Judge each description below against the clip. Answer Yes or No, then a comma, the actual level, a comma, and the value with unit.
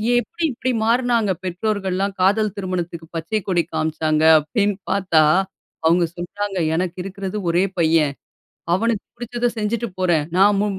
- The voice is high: Yes, high, 195 Hz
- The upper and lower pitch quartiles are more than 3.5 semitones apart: Yes, average, 3.9 semitones